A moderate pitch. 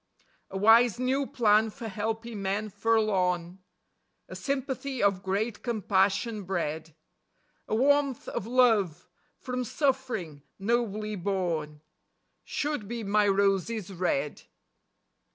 No: high, 210 Hz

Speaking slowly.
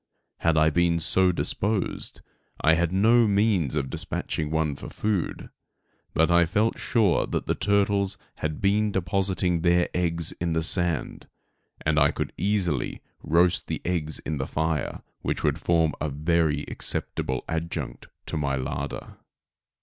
No: average, 150 wpm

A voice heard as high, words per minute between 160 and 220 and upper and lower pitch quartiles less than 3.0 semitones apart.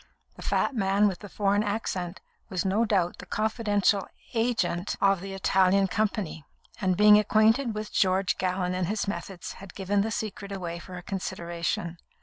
Yes: high, 195 Hz; average, 165 wpm; narrow, 2.4 semitones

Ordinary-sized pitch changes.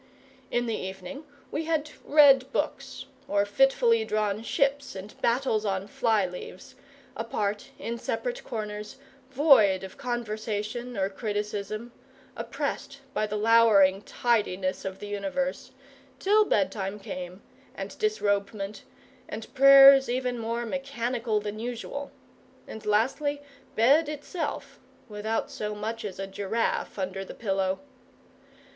Yes: average, 4.7 semitones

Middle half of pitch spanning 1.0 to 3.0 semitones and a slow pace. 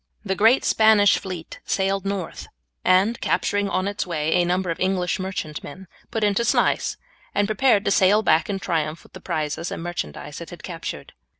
No: average, 2.7 semitones; average, 180 wpm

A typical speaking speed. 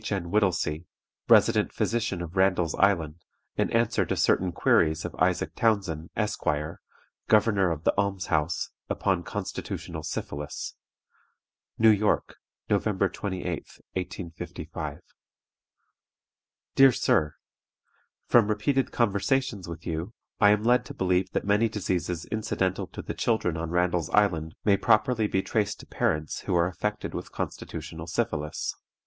No: slow, 130 wpm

